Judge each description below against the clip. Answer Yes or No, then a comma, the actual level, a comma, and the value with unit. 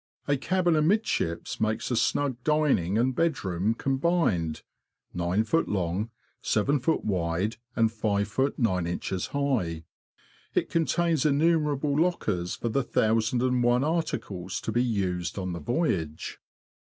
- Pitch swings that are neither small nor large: No, wide, 7.7 semitones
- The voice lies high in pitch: No, low, 115 Hz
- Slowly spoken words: Yes, slow, 120 wpm